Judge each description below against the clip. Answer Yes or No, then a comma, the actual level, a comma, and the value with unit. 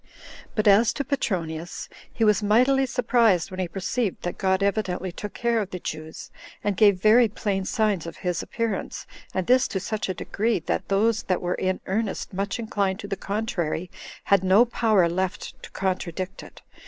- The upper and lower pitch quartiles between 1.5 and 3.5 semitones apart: Yes, average, 3.1 semitones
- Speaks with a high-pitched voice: Yes, high, 200 Hz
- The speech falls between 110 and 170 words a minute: No, average, 180 wpm